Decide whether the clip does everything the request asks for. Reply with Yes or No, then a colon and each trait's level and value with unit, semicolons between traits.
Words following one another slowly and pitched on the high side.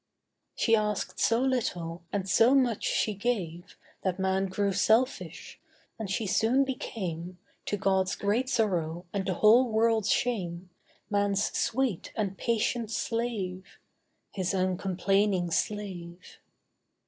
Yes: slow, 120 wpm; high, 200 Hz